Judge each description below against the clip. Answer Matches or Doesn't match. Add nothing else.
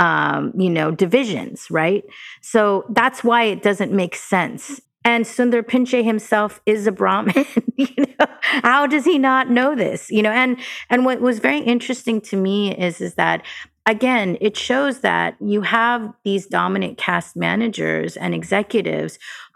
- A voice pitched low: Doesn't match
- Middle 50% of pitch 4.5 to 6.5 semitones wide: Doesn't match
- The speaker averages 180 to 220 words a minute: Doesn't match